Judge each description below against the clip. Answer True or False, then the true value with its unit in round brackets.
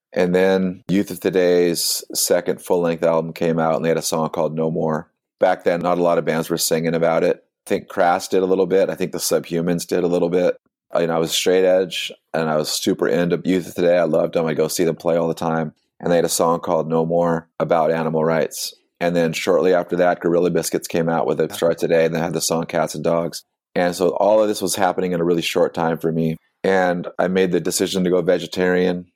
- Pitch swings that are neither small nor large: False (1.8 semitones)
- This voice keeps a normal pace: False (255 wpm)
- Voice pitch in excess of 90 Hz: False (85 Hz)